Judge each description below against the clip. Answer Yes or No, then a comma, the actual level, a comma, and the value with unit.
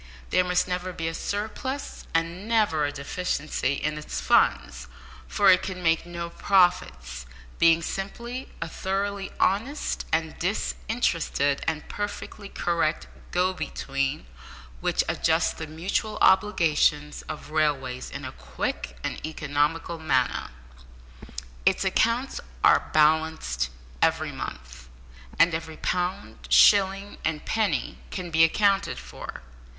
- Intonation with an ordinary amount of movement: Yes, average, 4.2 semitones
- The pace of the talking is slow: Yes, slow, 120 wpm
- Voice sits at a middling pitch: Yes, medium, 165 Hz